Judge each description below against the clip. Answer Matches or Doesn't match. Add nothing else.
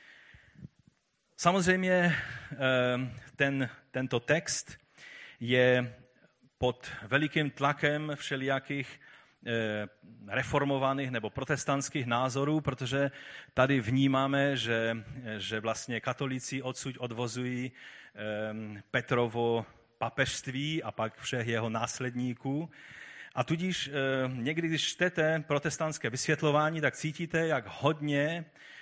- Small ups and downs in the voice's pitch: Doesn't match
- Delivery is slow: Matches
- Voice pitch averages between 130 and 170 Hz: Matches